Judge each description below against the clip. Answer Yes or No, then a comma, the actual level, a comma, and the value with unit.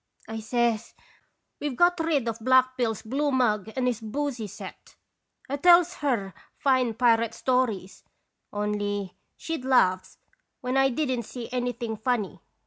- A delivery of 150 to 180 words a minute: No, average, 140 wpm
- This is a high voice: Yes, high, 245 Hz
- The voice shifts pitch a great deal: No, average, 3.4 semitones